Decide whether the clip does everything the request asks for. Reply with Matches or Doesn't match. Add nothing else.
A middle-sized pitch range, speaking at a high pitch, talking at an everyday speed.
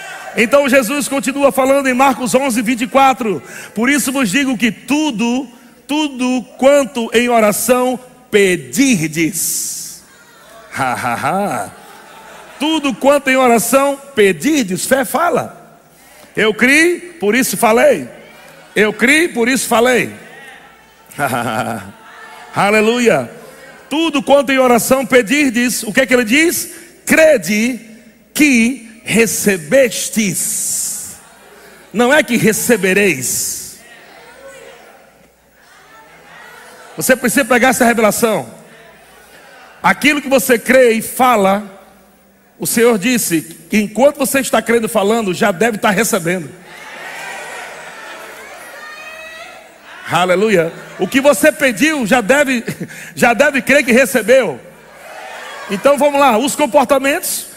Doesn't match